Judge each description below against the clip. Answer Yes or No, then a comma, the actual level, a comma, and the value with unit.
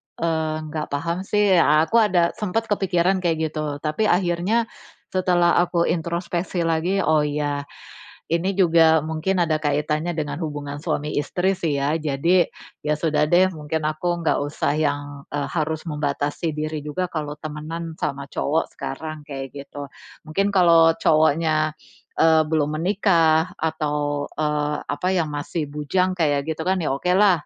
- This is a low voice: No, medium, 160 Hz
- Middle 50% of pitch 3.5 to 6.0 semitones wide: No, average, 2.8 semitones